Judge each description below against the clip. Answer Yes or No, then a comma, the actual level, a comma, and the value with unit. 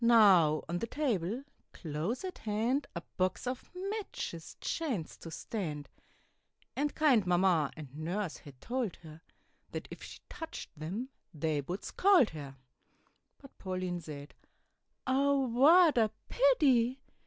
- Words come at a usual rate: No, slow, 130 wpm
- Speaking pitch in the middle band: No, high, 210 Hz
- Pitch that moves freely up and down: Yes, wide, 8.6 semitones